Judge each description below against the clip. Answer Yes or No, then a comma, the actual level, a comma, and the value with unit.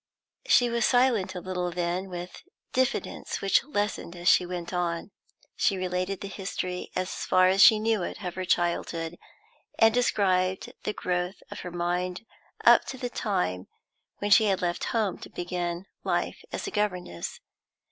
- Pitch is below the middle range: No, medium, 185 Hz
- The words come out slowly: No, average, 165 wpm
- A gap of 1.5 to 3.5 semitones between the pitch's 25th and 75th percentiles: Yes, average, 2.7 semitones